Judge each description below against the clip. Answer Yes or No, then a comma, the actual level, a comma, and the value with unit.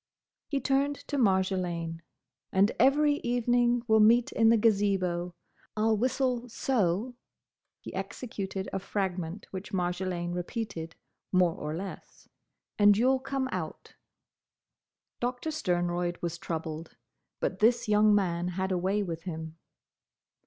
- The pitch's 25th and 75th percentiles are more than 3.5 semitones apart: Yes, average, 5.3 semitones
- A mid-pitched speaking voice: No, high, 195 Hz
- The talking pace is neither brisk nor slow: No, slow, 125 wpm